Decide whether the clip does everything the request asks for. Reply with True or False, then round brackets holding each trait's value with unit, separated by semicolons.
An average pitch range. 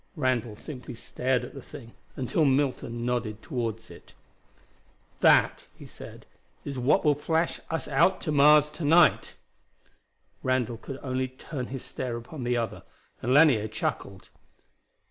True (3.7 semitones)